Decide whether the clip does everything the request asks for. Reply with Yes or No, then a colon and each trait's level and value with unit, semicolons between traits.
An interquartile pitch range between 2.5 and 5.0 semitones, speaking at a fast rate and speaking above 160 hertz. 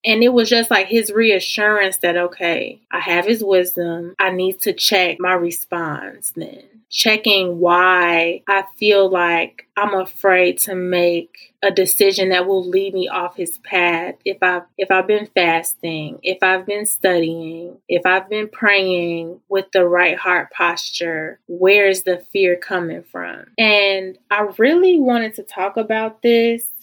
No: average, 2.9 semitones; average, 160 wpm; high, 190 Hz